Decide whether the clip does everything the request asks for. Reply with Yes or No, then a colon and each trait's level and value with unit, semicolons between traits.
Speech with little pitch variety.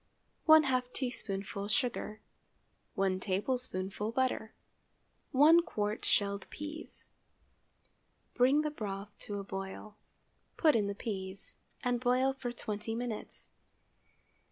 No: average, 4.3 semitones